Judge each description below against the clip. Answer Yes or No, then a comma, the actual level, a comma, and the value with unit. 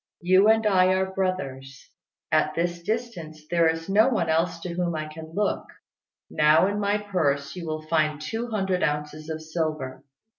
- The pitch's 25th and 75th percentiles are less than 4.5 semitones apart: Yes, average, 3.7 semitones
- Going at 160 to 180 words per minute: Yes, average, 175 wpm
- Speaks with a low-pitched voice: No, medium, 170 Hz